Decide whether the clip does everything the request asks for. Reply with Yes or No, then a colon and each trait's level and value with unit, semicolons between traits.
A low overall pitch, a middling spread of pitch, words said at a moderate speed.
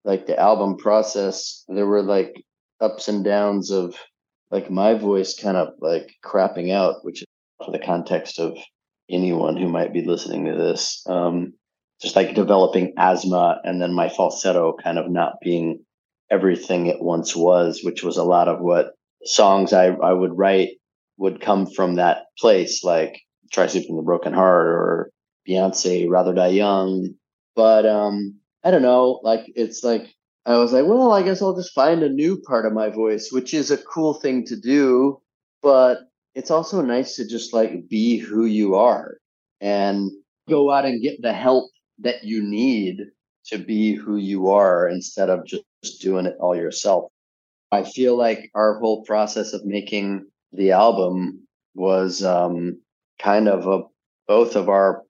Yes: low, 100 Hz; average, 3.9 semitones; average, 170 wpm